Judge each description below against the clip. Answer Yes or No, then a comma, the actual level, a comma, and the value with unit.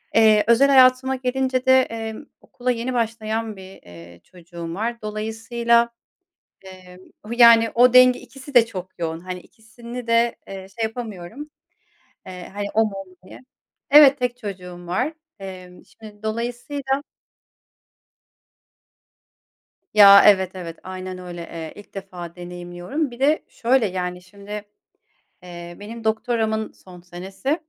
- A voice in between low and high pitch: No, high, 220 Hz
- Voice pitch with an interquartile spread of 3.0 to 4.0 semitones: No, average, 4.8 semitones